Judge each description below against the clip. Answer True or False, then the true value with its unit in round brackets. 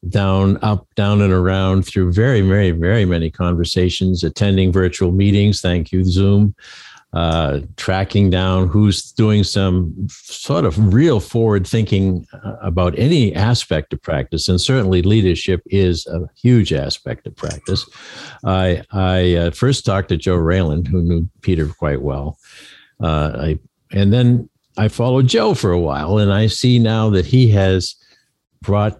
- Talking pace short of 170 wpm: True (150 wpm)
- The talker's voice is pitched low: True (95 Hz)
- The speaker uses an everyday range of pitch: True (3.0 semitones)